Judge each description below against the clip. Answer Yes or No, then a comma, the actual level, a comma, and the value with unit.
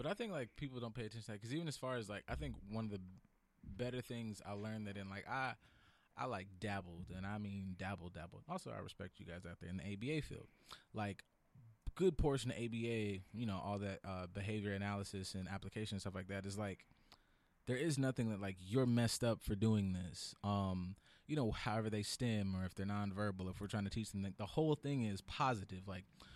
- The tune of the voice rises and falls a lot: No, average, 3.2 semitones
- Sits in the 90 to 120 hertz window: Yes, low, 100 Hz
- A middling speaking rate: No, fast, 235 wpm